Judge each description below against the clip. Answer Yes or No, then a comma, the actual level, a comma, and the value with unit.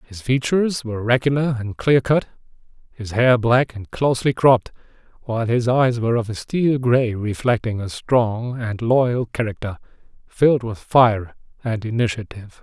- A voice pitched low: Yes, low, 120 Hz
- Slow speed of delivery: No, average, 150 wpm